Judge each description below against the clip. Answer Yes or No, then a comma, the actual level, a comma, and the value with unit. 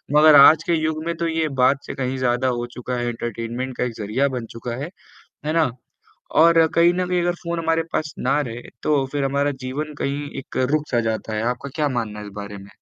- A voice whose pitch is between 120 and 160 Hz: Yes, medium, 140 Hz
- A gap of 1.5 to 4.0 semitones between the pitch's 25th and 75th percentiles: No, average, 4.6 semitones